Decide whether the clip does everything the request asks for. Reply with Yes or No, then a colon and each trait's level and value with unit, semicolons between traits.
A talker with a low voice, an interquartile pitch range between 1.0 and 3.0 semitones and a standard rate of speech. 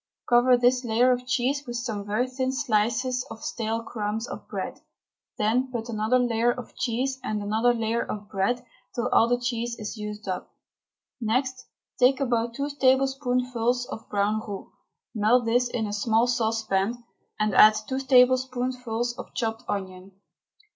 No: high, 240 Hz; narrow, 2.4 semitones; average, 155 wpm